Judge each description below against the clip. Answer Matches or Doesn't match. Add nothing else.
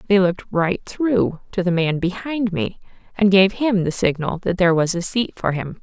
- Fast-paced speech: Matches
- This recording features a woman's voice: Matches